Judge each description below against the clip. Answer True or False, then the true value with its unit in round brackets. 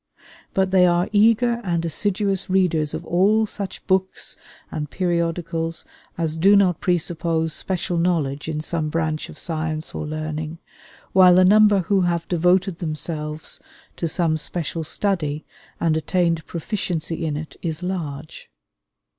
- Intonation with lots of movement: False (3.0 semitones)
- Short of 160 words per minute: True (140 wpm)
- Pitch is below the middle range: False (170 Hz)